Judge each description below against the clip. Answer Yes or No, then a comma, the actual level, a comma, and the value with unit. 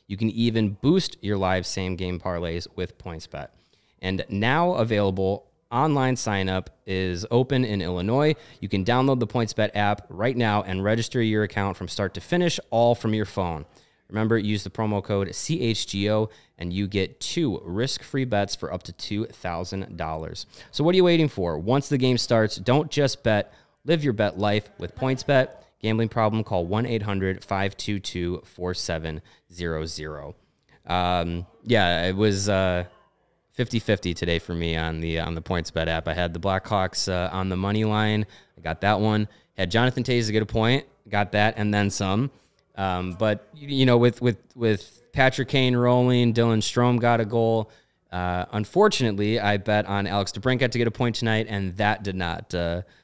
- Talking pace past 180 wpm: No, average, 175 wpm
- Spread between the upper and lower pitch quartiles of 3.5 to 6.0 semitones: Yes, average, 4.2 semitones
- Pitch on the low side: Yes, low, 105 Hz